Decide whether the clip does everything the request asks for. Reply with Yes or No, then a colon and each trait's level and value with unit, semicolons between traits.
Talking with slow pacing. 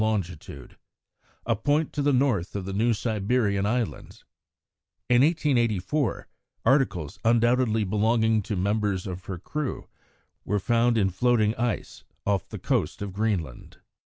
Yes: slow, 130 wpm